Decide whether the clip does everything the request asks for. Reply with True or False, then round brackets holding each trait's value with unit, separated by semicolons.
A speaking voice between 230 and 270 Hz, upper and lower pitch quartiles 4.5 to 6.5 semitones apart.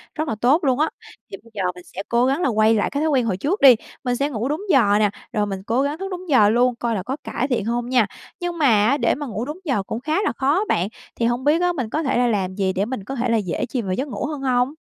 True (245 Hz; 5.1 semitones)